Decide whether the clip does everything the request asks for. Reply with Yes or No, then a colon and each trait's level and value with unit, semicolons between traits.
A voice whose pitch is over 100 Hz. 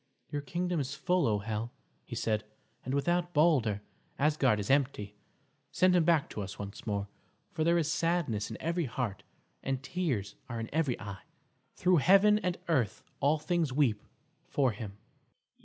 Yes: medium, 140 Hz